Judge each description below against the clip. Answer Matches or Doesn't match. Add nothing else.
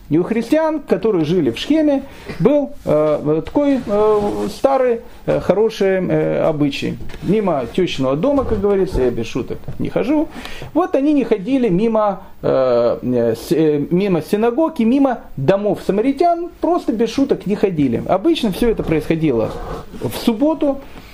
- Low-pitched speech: Doesn't match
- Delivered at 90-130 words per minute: Doesn't match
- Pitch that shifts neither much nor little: Doesn't match